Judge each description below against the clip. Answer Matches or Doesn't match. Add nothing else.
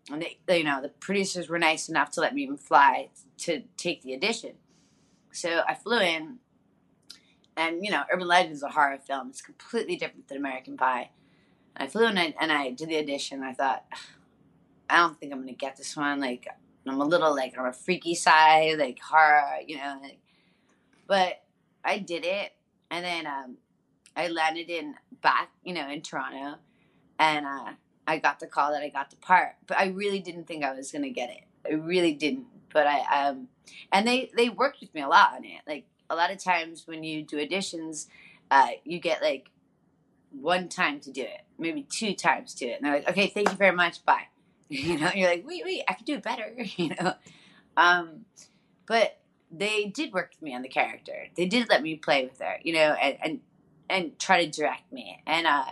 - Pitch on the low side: Doesn't match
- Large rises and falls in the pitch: Matches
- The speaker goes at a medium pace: Doesn't match